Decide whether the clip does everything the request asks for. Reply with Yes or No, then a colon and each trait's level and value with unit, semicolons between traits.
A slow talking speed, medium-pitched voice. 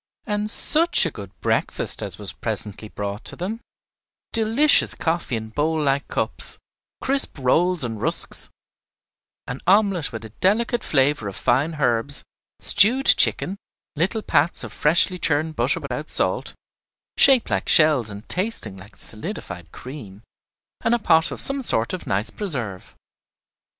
No: average, 145 wpm; medium, 155 Hz